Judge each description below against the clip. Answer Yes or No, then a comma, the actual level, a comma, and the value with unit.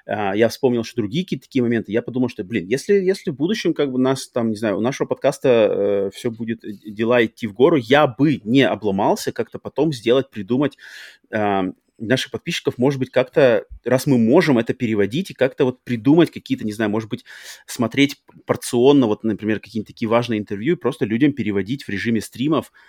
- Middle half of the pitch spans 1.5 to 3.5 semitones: No, average, 3.9 semitones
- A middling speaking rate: No, fast, 195 wpm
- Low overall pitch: Yes, low, 120 Hz